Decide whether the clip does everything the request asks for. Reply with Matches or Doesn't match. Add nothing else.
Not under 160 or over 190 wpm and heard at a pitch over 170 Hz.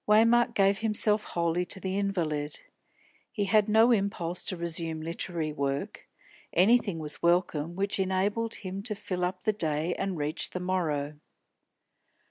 Doesn't match